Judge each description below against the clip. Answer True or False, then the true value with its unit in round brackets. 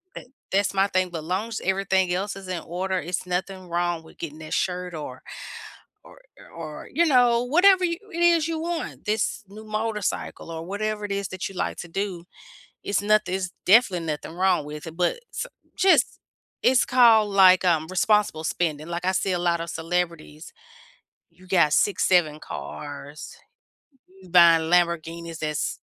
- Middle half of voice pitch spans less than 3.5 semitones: False (3.8 semitones)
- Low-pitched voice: False (185 Hz)